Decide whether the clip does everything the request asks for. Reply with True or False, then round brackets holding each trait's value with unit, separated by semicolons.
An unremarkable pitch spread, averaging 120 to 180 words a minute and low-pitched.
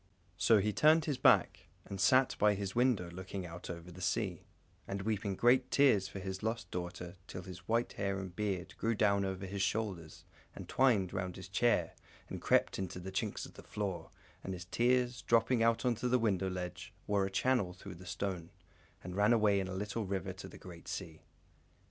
False (3.6 semitones; 200 wpm; 100 Hz)